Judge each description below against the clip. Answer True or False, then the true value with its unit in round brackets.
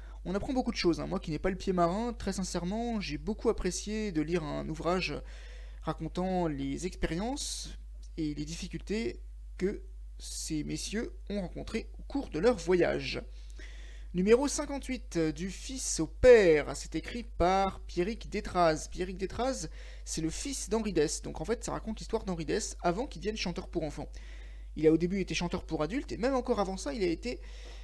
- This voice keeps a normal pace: True (185 wpm)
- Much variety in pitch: True (5.7 semitones)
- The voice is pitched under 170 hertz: False (180 Hz)